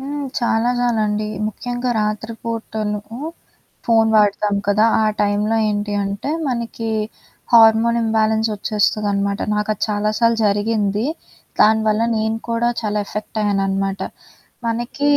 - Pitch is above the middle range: Yes, high, 215 Hz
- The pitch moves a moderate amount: No, narrow, 1.8 semitones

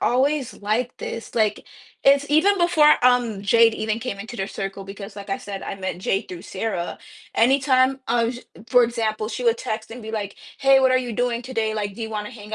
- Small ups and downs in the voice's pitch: No, average, 3.4 semitones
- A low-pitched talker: No, high, 230 Hz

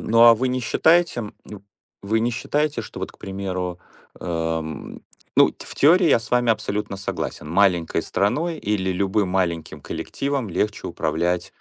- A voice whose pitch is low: Yes, low, 105 Hz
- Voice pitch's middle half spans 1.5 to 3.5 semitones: No, average, 5.0 semitones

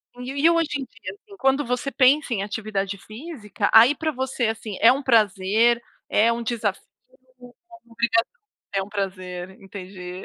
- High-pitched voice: Yes, high, 235 Hz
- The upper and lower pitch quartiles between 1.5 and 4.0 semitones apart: No, average, 4.8 semitones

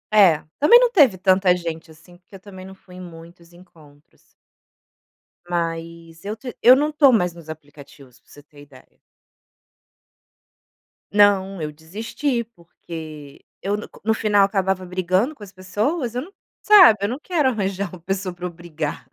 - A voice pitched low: No, medium, 185 Hz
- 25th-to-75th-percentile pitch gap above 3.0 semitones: Yes, average, 4.4 semitones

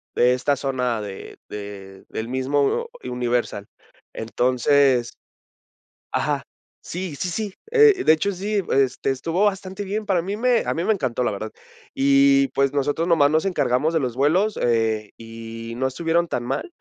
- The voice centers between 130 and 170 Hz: Yes, medium, 140 Hz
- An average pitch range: No, wide, 6.8 semitones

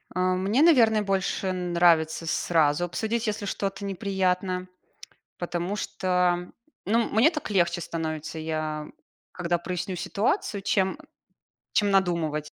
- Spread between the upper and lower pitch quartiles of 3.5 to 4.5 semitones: No, average, 2.8 semitones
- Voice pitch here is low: No, medium, 185 Hz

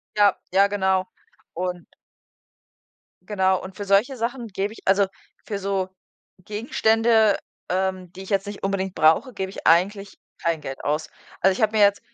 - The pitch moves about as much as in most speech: No, narrow, 1.9 semitones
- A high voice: Yes, high, 195 Hz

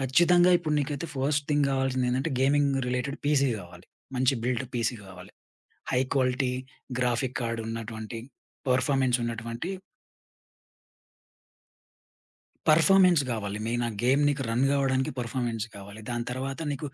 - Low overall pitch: Yes, low, 130 Hz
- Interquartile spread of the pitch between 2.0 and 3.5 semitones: Yes, average, 3.1 semitones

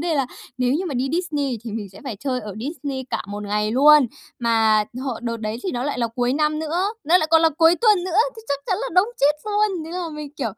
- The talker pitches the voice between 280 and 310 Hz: Yes, very high, 290 Hz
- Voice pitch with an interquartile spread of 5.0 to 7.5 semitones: Yes, wide, 5.6 semitones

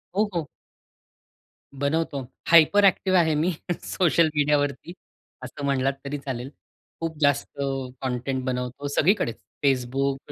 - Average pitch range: Yes, average, 3.5 semitones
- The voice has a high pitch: No, medium, 145 Hz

